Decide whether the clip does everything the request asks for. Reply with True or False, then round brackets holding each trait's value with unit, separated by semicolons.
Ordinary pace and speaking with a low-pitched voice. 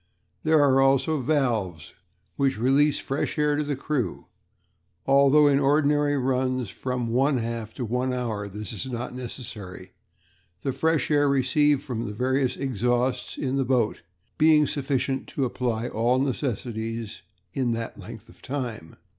True (150 wpm; 130 Hz)